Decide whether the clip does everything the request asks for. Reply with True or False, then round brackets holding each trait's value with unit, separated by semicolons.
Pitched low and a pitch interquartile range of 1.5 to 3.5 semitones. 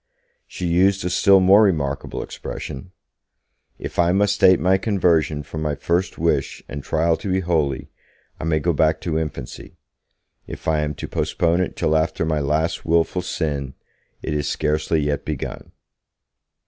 True (80 Hz; 3.1 semitones)